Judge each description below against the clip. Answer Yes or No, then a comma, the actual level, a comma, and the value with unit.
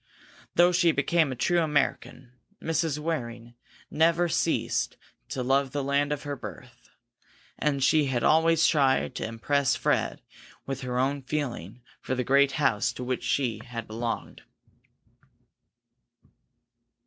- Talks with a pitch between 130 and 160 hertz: Yes, medium, 140 Hz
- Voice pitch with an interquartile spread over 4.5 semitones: No, average, 3.5 semitones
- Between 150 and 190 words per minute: No, average, 140 wpm